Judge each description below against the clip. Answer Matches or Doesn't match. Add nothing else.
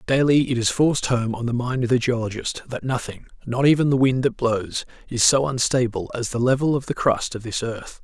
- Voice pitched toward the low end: Matches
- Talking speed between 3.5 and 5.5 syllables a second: Matches